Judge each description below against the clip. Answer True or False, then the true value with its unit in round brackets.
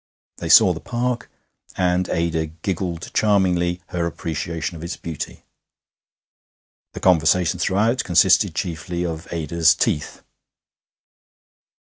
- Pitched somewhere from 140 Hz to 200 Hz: False (85 Hz)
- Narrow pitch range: True (2.1 semitones)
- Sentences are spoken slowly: True (105 wpm)